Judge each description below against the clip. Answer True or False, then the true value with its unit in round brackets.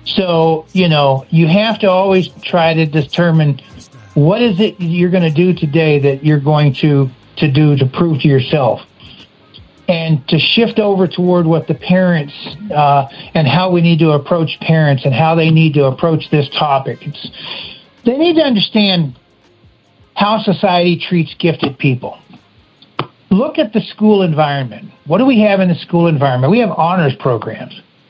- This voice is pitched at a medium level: True (165 Hz)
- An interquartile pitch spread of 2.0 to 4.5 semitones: True (4.2 semitones)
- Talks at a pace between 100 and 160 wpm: False (170 wpm)